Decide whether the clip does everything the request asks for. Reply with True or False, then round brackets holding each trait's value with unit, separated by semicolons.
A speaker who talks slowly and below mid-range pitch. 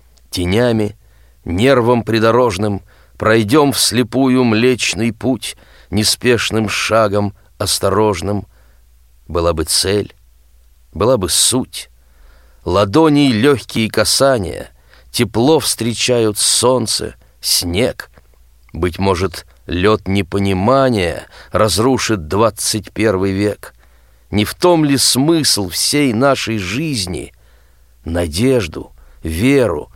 True (80 wpm; 100 Hz)